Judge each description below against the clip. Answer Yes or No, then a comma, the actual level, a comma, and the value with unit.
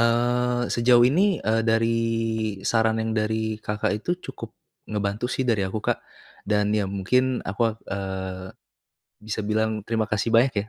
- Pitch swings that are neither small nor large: No, narrow, 2.3 semitones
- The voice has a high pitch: No, low, 110 Hz